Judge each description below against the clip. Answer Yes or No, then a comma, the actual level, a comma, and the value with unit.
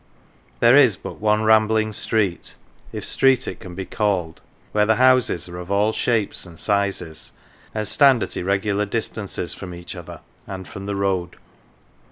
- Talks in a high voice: No, low, 100 Hz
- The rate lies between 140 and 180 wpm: Yes, average, 165 wpm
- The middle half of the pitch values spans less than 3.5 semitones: Yes, average, 2.8 semitones